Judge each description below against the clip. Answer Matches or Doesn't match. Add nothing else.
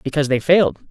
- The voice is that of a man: Matches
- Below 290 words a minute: Matches